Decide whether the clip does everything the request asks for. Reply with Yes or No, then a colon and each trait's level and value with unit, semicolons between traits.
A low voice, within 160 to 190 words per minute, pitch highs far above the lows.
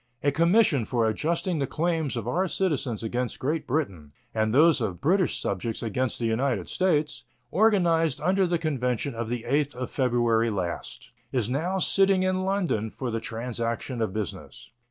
Yes: low, 130 Hz; average, 165 wpm; wide, 6.6 semitones